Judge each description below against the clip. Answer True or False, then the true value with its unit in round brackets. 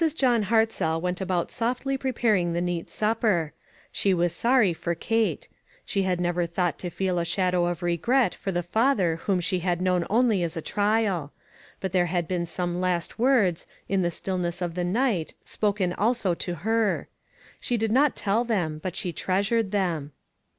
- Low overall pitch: False (185 Hz)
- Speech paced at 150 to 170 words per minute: False (180 wpm)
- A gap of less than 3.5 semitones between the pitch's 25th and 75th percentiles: False (4.1 semitones)